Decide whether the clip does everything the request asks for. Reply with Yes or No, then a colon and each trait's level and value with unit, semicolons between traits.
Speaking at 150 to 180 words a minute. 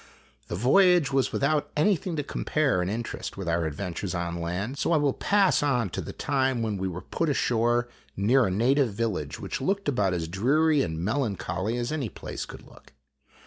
No: average, 190 wpm